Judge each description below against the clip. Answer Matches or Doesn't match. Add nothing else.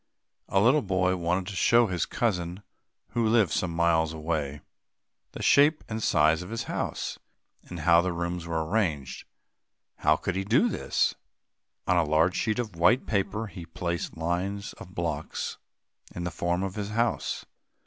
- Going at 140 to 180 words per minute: Matches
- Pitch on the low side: Matches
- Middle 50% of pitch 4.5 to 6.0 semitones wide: Doesn't match